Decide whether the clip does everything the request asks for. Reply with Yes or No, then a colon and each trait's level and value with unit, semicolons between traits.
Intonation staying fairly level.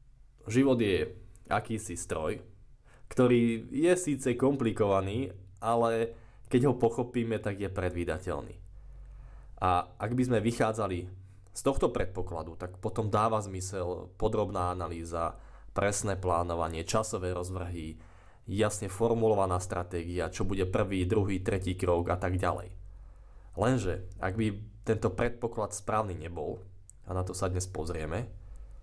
No: average, 3.9 semitones